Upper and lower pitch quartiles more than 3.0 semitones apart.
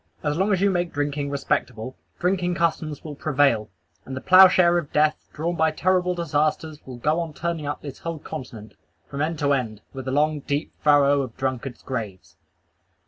Yes: average, 3.9 semitones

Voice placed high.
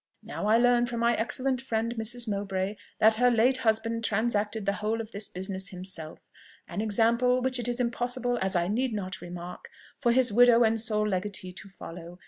Yes: high, 220 Hz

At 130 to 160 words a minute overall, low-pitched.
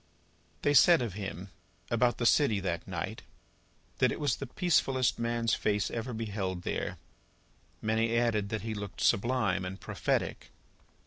Yes: average, 145 wpm; low, 110 Hz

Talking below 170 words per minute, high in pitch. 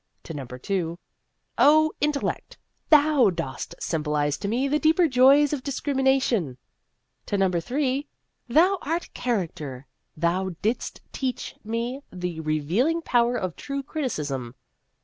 Yes: average, 150 wpm; high, 235 Hz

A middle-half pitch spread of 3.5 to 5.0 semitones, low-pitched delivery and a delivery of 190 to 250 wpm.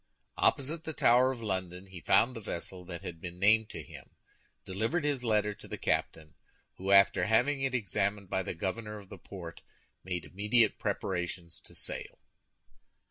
No: average, 4.0 semitones; low, 100 Hz; average, 170 wpm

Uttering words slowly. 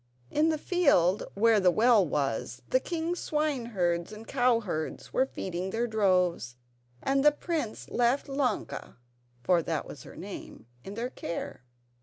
No: average, 145 wpm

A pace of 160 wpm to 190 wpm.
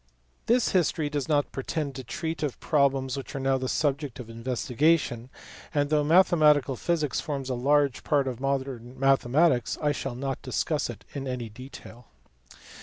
Yes: average, 170 wpm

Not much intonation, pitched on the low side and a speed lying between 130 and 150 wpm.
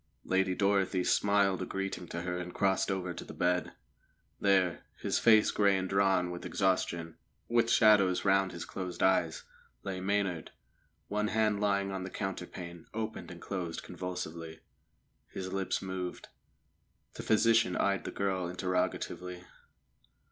Yes: narrow, 1.7 semitones; very low, 95 Hz; average, 140 wpm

